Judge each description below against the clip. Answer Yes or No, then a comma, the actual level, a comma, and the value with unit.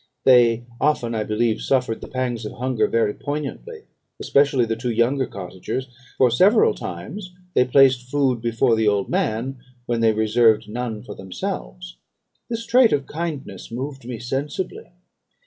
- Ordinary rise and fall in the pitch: Yes, average, 3.7 semitones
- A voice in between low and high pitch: No, low, 120 Hz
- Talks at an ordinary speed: Yes, average, 150 wpm